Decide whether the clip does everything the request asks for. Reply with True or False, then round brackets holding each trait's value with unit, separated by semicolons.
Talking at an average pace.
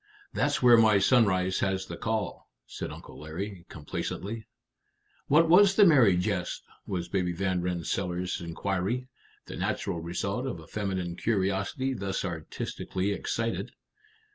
False (130 wpm)